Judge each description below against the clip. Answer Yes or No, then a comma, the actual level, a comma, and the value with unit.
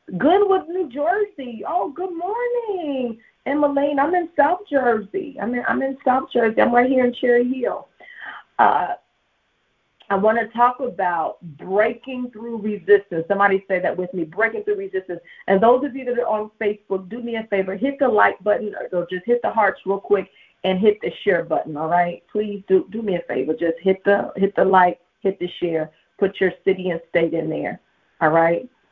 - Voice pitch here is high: Yes, high, 210 Hz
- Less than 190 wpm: No, average, 195 wpm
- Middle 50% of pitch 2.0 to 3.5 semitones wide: No, average, 5.3 semitones